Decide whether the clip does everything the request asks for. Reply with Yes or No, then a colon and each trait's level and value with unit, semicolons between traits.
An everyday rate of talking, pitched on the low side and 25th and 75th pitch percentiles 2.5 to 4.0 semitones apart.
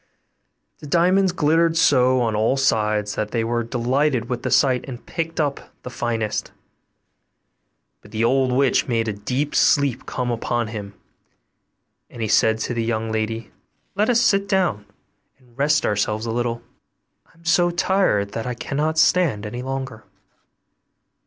No: average, 160 wpm; low, 125 Hz; average, 4.9 semitones